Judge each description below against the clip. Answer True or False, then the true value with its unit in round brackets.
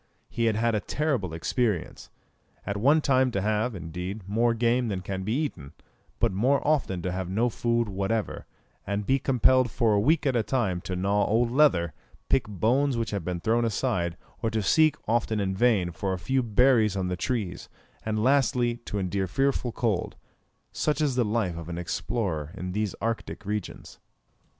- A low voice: True (110 Hz)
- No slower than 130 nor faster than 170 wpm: False (185 wpm)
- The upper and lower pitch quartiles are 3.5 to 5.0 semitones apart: True (4.5 semitones)